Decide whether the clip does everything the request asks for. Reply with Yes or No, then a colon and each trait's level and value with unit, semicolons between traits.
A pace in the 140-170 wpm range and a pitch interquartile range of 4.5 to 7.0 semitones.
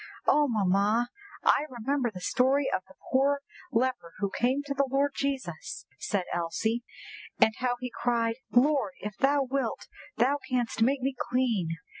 No: average, 160 wpm; average, 3.8 semitones